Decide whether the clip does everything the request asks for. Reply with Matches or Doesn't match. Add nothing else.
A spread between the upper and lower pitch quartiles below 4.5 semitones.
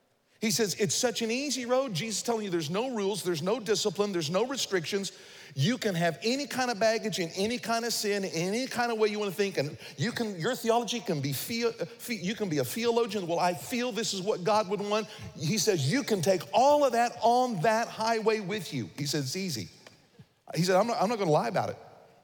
Matches